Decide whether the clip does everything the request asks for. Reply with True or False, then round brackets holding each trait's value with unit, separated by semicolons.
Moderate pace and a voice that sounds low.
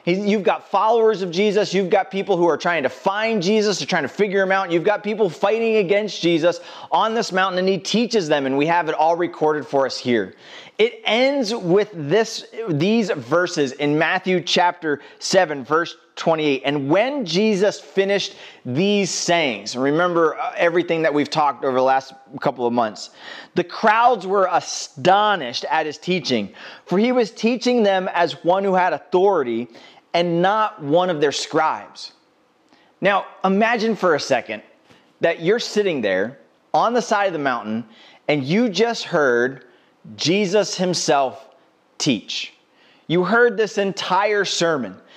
False (160 wpm; 180 Hz)